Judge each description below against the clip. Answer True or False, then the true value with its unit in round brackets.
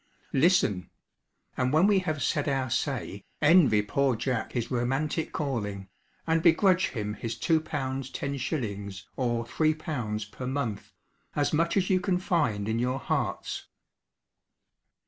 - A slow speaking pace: True (130 wpm)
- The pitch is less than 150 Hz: True (135 Hz)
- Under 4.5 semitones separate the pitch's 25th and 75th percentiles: False (5.6 semitones)